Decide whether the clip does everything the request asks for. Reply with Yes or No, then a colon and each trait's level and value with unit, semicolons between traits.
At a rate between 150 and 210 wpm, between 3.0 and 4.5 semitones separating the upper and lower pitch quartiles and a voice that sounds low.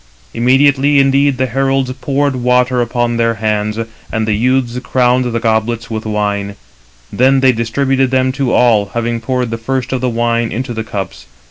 No: average, 170 wpm; narrow, 2.5 semitones; low, 125 Hz